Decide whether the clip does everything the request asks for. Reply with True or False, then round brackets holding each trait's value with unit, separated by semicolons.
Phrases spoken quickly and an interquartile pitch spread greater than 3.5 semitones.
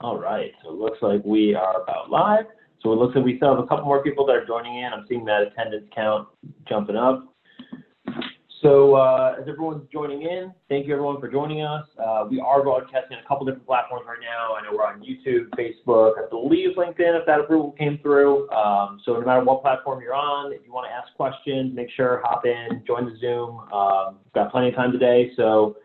True (230 wpm; 4.4 semitones)